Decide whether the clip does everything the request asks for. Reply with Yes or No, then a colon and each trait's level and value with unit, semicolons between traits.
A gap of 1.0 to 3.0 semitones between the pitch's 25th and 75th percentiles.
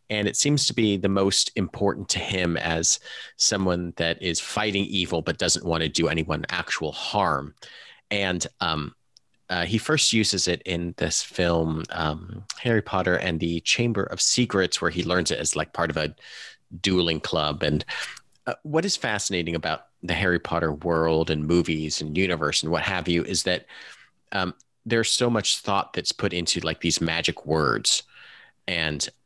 No: average, 3.4 semitones